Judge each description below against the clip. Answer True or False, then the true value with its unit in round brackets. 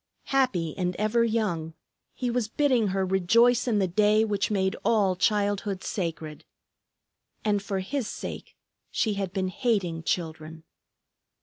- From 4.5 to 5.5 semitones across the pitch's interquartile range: False (3.7 semitones)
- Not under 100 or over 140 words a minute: True (135 wpm)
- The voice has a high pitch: True (200 Hz)